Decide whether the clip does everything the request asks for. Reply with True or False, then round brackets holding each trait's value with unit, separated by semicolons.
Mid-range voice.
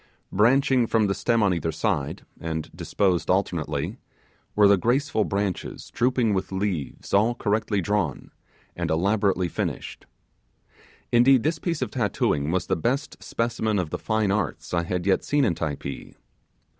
False (100 Hz)